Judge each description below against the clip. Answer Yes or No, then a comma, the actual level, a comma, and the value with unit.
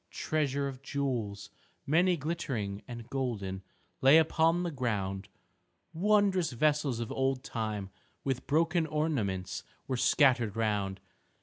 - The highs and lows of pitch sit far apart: Yes, wide, 6.4 semitones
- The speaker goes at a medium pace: No, slow, 115 wpm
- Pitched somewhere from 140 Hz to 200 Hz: No, low, 130 Hz